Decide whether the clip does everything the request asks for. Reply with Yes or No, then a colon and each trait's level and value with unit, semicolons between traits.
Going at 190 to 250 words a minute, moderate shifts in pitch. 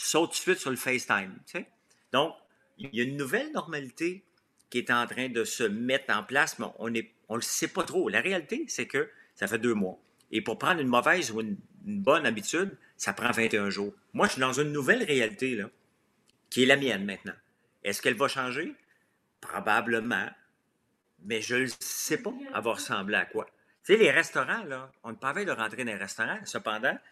No: average, 210 wpm; wide, 6.8 semitones